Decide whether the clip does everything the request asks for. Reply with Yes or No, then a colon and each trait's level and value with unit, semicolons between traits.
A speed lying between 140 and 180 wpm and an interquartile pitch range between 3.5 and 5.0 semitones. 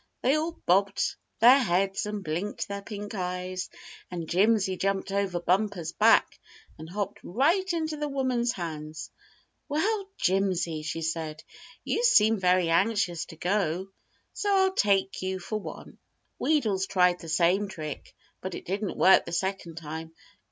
Yes: average, 150 wpm; average, 4.0 semitones